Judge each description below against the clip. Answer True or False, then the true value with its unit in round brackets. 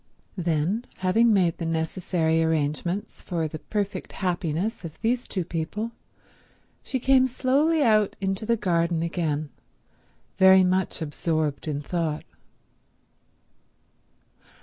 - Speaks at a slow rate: True (110 wpm)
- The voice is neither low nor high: True (180 Hz)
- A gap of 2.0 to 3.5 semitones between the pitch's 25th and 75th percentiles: False (4.8 semitones)